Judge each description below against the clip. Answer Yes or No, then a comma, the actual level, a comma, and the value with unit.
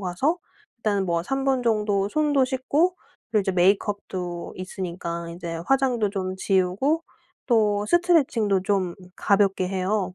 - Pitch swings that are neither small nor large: No, wide, 5.8 semitones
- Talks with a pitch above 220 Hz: No, high, 200 Hz